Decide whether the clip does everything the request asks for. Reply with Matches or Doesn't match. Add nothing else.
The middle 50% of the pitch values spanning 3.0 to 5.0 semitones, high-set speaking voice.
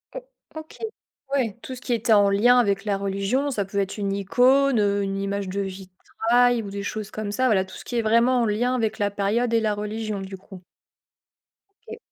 Matches